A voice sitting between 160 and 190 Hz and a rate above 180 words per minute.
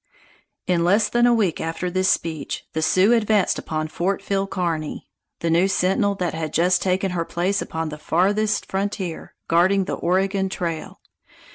No: medium, 185 Hz; average, 165 wpm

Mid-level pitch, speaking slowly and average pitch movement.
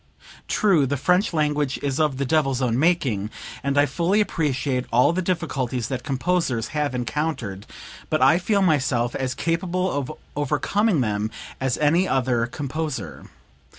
No: medium, 145 Hz; average, 150 wpm; average, 4.6 semitones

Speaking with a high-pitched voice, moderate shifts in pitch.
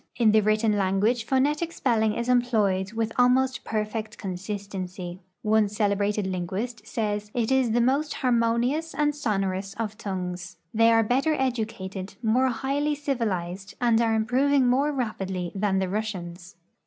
Yes: high, 220 Hz; average, 4.1 semitones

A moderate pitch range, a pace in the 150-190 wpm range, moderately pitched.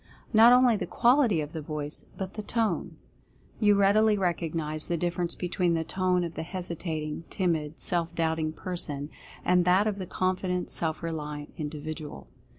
Yes: average, 3.2 semitones; average, 160 wpm; medium, 175 Hz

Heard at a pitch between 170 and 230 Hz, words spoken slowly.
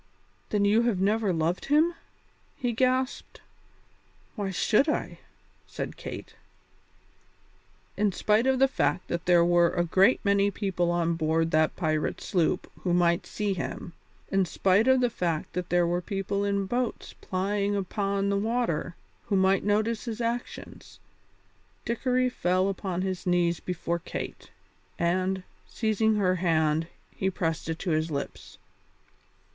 No: high, 190 Hz; average, 145 wpm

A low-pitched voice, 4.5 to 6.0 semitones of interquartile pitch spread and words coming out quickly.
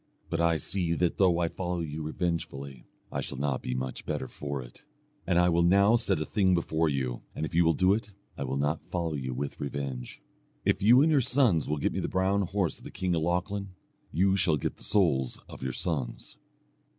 Yes: very low, 85 Hz; average, 4.8 semitones; fast, 225 wpm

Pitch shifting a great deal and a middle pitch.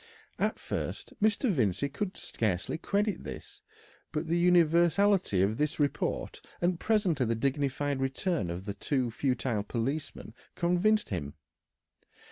Yes: wide, 7.2 semitones; medium, 145 Hz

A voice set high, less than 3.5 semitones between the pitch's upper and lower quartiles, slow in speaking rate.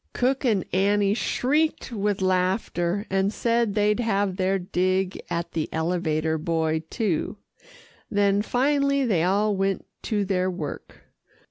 Yes: high, 195 Hz; average, 2.9 semitones; slow, 130 wpm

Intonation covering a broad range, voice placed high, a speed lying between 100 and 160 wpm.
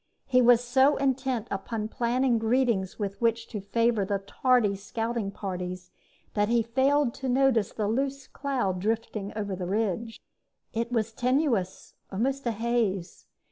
No: average, 3.9 semitones; high, 230 Hz; average, 145 wpm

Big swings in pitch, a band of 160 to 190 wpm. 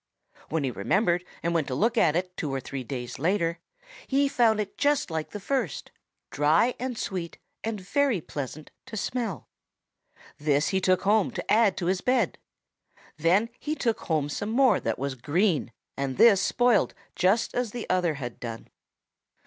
Yes: wide, 7.2 semitones; average, 175 wpm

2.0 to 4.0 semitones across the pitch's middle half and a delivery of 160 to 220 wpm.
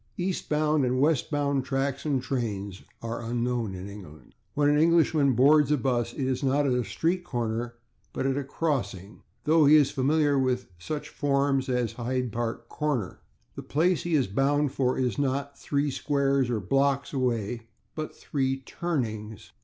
Yes: average, 3.4 semitones; average, 165 wpm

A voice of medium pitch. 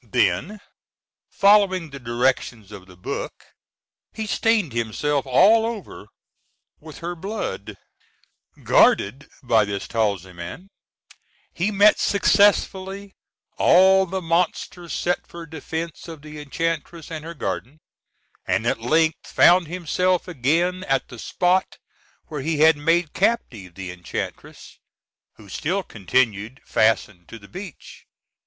Yes: medium, 160 Hz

